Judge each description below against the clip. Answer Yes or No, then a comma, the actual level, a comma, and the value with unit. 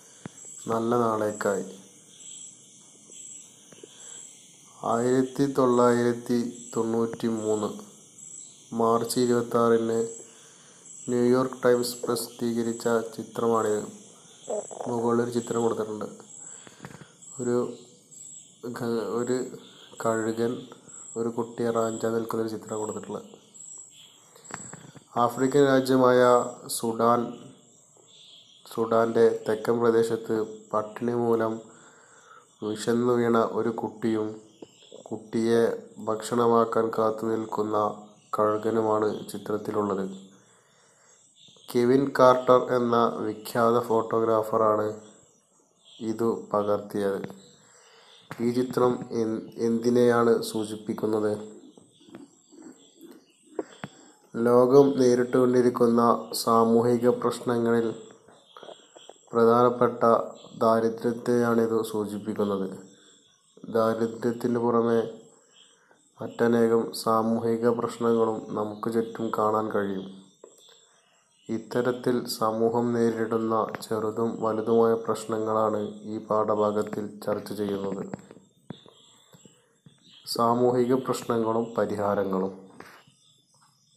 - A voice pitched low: Yes, low, 115 Hz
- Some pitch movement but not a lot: No, narrow, 1.6 semitones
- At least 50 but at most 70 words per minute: Yes, slow, 60 wpm